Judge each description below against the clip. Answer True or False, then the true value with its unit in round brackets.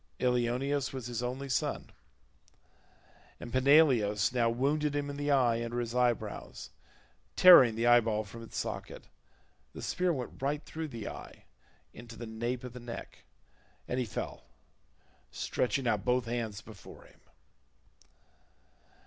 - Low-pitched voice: True (125 Hz)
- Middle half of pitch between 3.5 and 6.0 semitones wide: False (2.8 semitones)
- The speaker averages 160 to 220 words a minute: False (140 wpm)